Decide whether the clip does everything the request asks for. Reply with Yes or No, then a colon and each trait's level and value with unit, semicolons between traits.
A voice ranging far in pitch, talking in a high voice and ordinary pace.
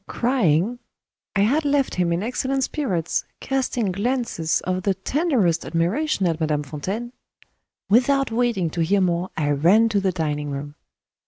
Yes: wide, 6.8 semitones; high, 195 Hz; average, 150 wpm